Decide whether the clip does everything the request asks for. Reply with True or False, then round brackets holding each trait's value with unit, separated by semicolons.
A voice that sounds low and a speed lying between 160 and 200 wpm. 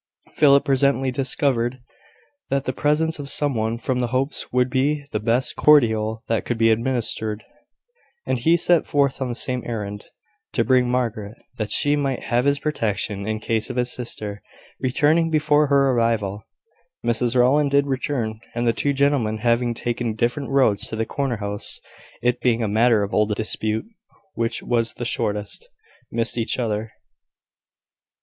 True (120 Hz; 165 wpm)